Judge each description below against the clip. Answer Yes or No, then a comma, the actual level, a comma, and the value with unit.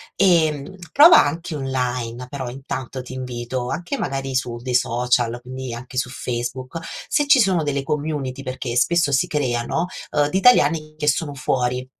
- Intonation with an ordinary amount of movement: Yes, average, 3.5 semitones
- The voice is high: No, low, 135 Hz